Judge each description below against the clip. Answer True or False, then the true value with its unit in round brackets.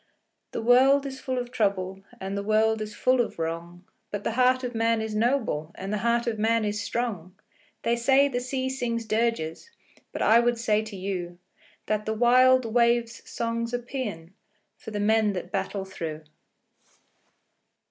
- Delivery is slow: False (175 wpm)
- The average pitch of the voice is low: False (225 Hz)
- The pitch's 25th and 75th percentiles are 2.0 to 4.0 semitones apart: True (3.3 semitones)